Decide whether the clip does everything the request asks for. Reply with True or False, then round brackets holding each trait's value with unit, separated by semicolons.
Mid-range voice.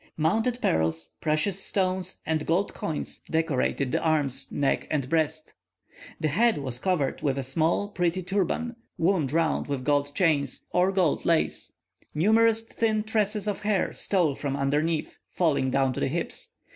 True (160 Hz)